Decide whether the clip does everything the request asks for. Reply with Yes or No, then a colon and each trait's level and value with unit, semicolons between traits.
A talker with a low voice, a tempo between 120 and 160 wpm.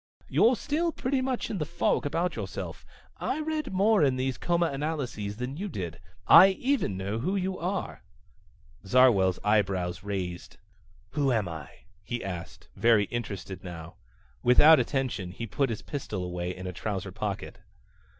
Yes: low, 120 Hz; average, 150 wpm